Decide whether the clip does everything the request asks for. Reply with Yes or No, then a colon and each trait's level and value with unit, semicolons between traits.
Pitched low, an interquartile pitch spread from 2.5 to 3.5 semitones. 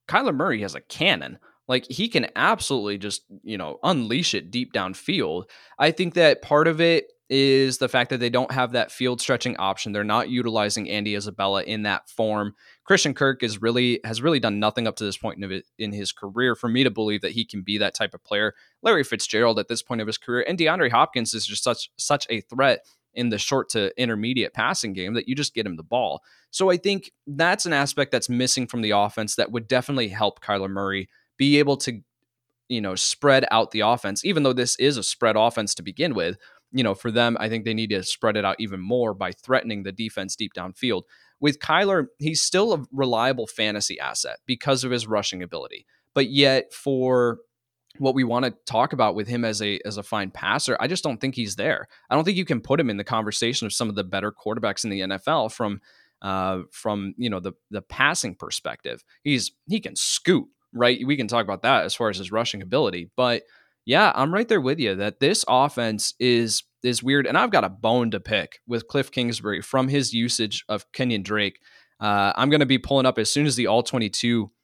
No: low, 120 Hz; average, 4.0 semitones